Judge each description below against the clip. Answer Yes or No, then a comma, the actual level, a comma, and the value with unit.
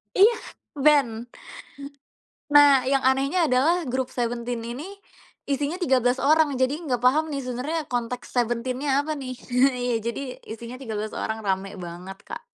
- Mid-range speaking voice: No, very high, 255 Hz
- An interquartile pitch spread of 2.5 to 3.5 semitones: Yes, average, 3.2 semitones